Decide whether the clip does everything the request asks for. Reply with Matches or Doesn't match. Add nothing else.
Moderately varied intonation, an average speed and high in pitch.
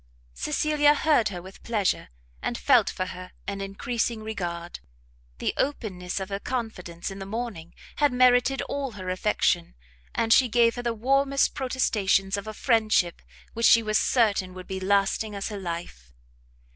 Matches